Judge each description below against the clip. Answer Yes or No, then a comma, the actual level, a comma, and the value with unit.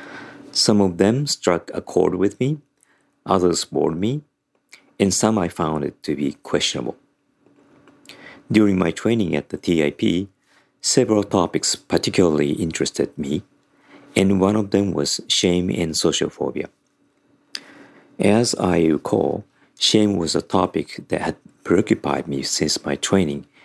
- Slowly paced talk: Yes, slow, 130 wpm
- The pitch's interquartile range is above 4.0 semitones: Yes, average, 4.5 semitones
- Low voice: Yes, low, 100 Hz